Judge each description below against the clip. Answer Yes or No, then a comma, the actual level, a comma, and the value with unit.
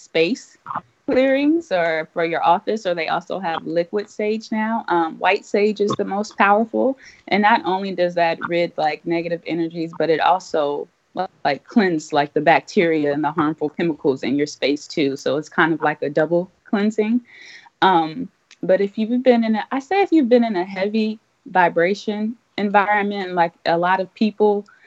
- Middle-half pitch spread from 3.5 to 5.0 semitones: Yes, average, 4.6 semitones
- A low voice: No, medium, 185 Hz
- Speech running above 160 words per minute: Yes, average, 180 wpm